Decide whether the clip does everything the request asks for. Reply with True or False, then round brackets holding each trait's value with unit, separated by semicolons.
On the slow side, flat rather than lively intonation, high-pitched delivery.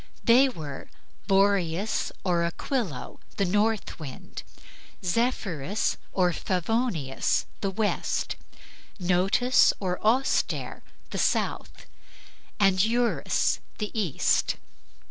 False (85 wpm; 4.2 semitones; 195 Hz)